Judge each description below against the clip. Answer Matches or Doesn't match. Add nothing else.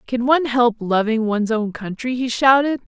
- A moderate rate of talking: Matches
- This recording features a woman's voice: Matches